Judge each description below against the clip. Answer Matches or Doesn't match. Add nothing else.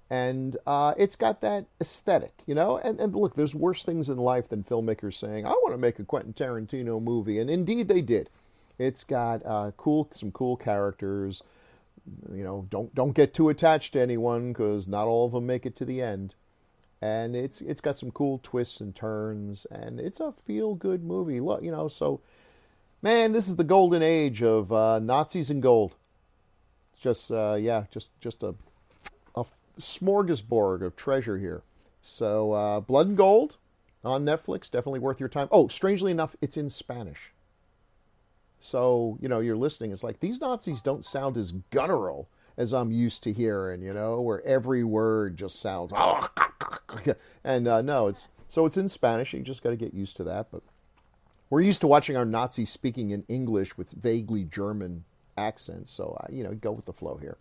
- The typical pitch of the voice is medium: Doesn't match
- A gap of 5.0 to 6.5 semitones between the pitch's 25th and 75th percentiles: Matches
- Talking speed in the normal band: Matches